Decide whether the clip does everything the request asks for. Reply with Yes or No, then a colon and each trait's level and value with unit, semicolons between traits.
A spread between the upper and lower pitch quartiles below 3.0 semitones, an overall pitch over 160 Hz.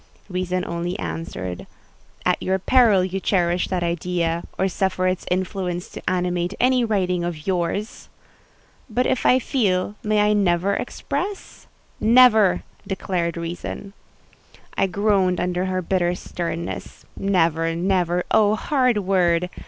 Yes: narrow, 2.6 semitones; medium, 185 Hz